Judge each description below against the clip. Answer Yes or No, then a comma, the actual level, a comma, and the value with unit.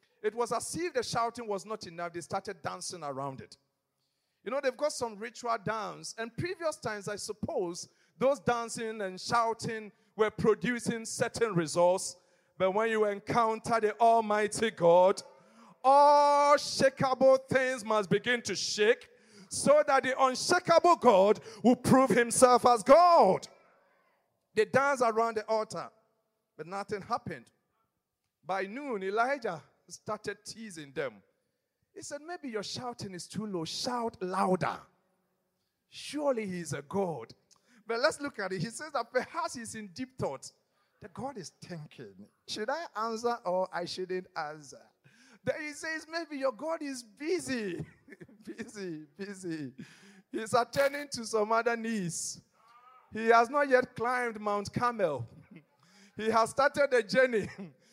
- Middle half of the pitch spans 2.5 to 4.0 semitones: No, average, 5.0 semitones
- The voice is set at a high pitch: Yes, high, 220 Hz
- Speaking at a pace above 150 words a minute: No, average, 145 wpm